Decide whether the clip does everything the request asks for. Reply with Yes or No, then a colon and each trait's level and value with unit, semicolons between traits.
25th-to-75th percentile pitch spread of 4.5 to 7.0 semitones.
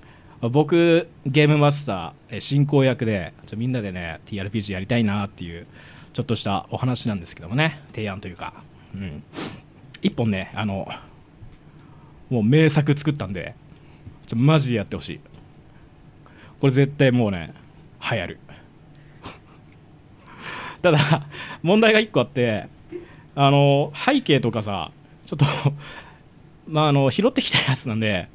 Yes: wide, 6.1 semitones